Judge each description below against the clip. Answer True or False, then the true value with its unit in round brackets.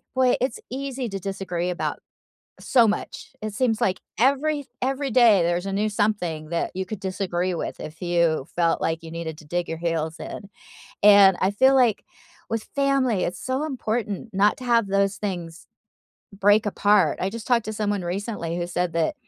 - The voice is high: True (200 Hz)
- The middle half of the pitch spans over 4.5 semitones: True (4.9 semitones)